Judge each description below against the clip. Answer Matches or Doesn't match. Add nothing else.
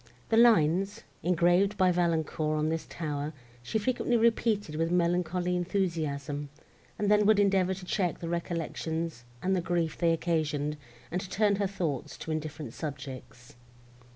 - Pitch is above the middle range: Doesn't match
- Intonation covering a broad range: Doesn't match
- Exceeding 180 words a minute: Doesn't match